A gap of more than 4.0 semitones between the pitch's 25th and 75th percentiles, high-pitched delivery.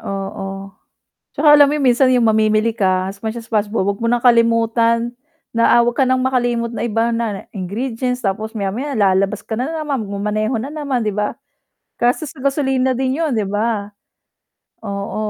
No: average, 3.6 semitones; high, 230 Hz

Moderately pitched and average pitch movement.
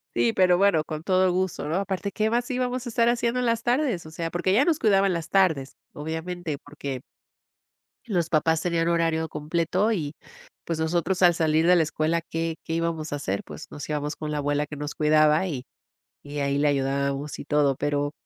Yes: medium, 165 Hz; average, 4.0 semitones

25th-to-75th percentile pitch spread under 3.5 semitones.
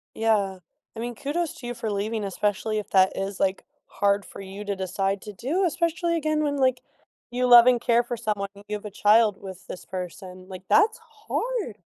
No: average, 4.3 semitones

